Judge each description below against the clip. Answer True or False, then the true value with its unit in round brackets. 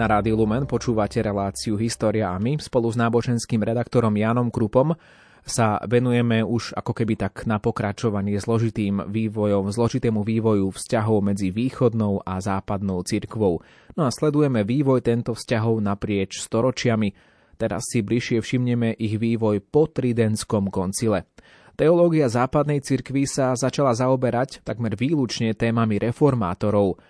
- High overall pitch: False (115 Hz)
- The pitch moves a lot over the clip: False (2.8 semitones)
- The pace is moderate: True (130 wpm)